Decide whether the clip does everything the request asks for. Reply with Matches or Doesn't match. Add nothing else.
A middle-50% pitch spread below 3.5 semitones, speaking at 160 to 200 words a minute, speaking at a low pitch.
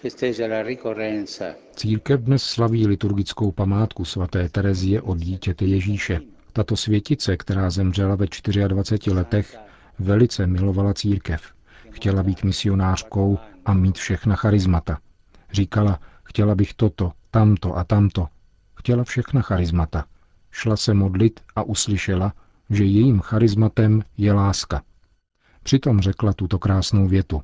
Doesn't match